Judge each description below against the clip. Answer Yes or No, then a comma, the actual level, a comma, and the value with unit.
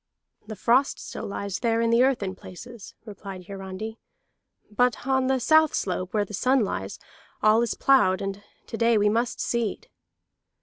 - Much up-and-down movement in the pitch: No, average, 3.7 semitones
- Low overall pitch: No, high, 220 Hz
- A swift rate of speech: No, average, 170 wpm